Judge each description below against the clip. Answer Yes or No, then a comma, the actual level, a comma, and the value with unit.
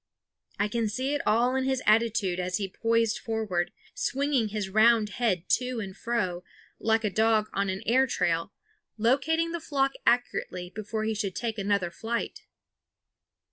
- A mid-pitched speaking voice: No, high, 220 Hz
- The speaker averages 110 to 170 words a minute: Yes, average, 160 wpm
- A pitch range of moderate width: Yes, average, 3.3 semitones